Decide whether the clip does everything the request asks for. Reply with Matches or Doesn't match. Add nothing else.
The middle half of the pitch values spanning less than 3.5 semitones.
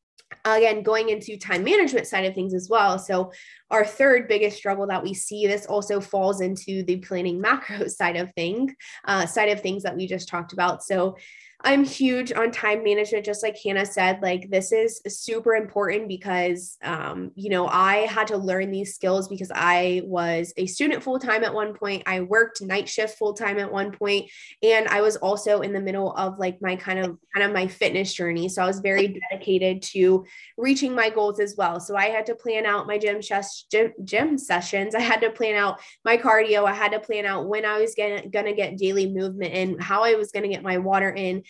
Matches